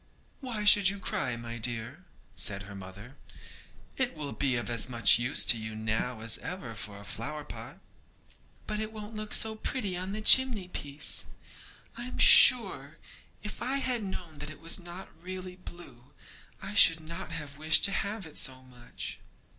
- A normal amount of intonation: No, wide, 8.6 semitones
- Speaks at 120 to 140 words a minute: No, average, 180 wpm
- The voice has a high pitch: No, medium, 160 Hz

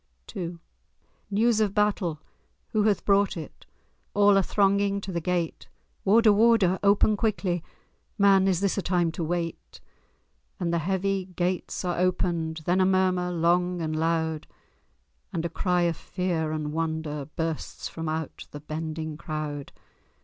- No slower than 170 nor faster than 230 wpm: No, average, 140 wpm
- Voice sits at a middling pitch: Yes, medium, 180 Hz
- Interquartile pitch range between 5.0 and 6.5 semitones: No, average, 3.3 semitones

